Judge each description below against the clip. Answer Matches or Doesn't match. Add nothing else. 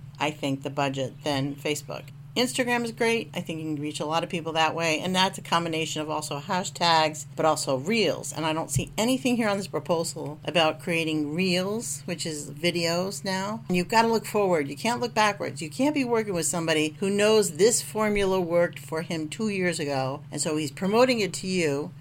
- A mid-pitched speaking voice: Matches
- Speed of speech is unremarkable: Doesn't match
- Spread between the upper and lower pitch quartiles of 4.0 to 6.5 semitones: Matches